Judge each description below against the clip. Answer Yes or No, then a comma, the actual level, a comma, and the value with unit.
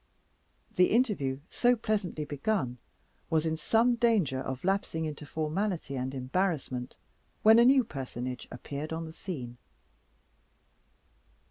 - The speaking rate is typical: No, slow, 120 wpm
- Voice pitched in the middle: Yes, medium, 160 Hz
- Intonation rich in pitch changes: Yes, wide, 7.8 semitones